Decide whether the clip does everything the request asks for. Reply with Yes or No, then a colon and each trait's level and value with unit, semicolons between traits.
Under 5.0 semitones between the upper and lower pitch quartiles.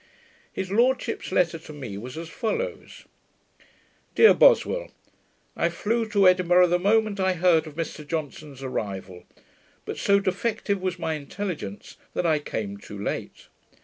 No: wide, 5.5 semitones